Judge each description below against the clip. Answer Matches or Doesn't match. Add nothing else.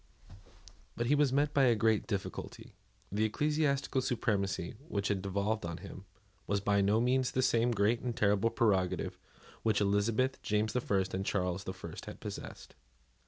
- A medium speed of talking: Matches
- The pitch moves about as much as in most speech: Matches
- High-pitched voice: Doesn't match